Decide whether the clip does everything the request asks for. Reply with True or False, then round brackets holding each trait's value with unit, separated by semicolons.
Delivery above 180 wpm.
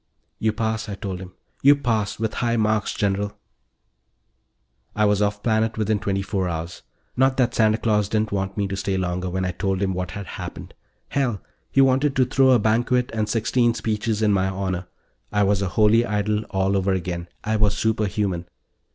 True (190 wpm)